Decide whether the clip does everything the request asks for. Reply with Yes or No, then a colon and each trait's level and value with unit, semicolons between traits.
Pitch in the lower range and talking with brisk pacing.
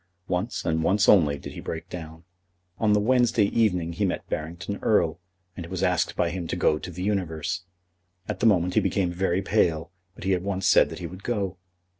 Yes: very low, 90 Hz; fast, 210 wpm